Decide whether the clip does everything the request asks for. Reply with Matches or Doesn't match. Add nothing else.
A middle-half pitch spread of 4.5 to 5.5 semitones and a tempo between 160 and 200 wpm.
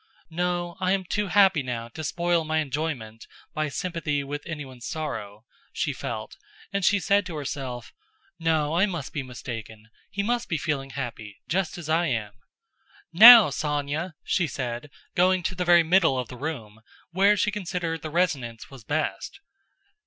Matches